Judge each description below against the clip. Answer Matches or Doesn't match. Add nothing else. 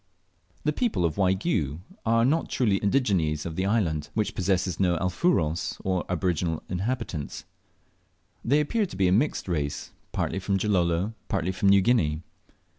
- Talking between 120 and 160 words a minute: Matches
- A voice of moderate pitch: Doesn't match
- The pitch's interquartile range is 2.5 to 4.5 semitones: Doesn't match